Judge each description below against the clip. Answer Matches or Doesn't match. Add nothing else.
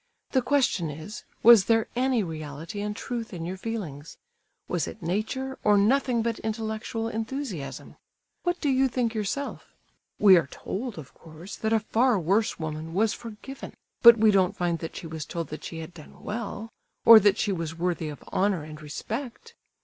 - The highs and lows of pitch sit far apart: Matches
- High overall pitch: Matches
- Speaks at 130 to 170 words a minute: Doesn't match